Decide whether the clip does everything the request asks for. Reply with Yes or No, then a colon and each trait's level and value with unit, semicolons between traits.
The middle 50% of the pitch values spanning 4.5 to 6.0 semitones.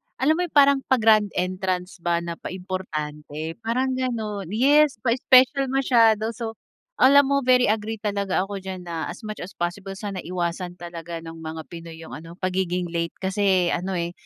Yes: average, 5.2 semitones